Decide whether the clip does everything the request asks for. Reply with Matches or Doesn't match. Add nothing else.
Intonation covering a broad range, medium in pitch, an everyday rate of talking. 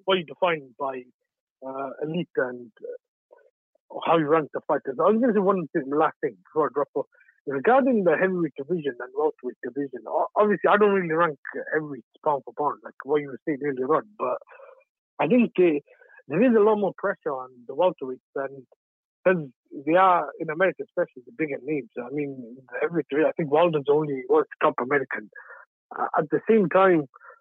Matches